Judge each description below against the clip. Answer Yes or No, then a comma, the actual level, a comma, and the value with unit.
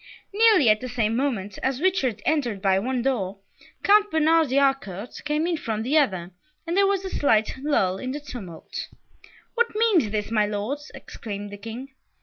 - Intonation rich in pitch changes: Yes, wide, 6.8 semitones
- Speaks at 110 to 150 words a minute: No, average, 180 wpm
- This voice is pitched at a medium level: No, very high, 255 Hz